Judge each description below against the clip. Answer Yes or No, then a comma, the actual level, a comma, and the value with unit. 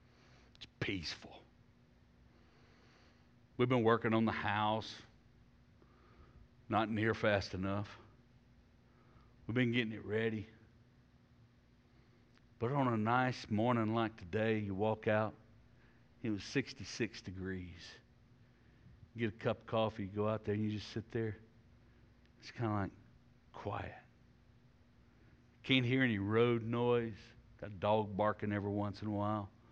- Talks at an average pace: No, slow, 130 wpm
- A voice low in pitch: Yes, low, 110 Hz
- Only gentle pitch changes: Yes, narrow, 2.2 semitones